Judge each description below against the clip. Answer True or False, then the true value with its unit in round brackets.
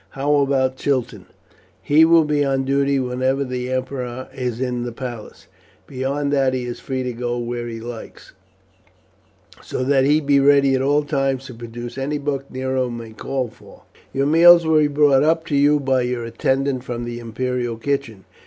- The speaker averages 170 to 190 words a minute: True (185 wpm)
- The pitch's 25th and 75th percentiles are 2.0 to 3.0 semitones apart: True (2.4 semitones)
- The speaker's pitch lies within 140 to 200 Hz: False (130 Hz)